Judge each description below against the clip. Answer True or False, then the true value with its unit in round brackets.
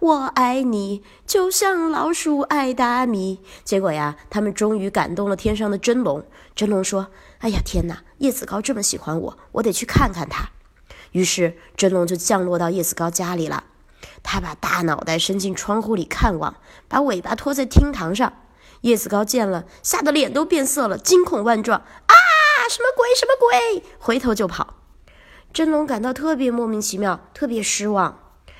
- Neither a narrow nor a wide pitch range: False (6.9 semitones)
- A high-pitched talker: True (225 Hz)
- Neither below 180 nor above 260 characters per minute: True (255 characters per minute)